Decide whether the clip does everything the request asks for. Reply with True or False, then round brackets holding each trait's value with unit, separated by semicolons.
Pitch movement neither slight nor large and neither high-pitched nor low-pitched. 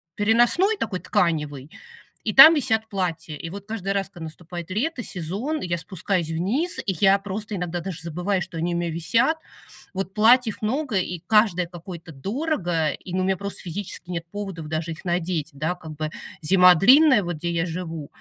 True (4.0 semitones; 180 Hz)